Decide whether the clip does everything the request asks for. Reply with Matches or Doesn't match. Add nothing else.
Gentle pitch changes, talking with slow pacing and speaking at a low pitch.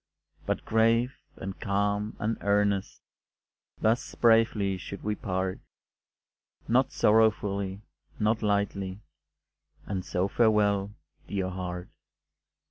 Matches